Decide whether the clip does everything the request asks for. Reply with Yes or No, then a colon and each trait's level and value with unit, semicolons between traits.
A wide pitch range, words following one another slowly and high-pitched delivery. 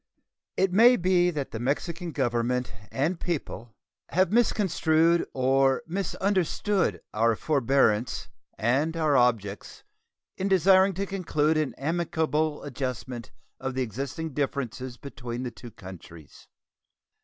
No: wide, 5.8 semitones; slow, 115 wpm; medium, 145 Hz